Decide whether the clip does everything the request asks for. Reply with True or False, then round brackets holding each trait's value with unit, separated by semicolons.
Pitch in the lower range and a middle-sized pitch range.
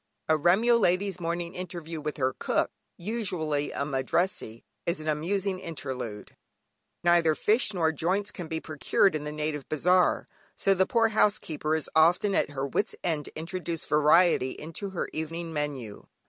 False (165 Hz; 3.4 semitones)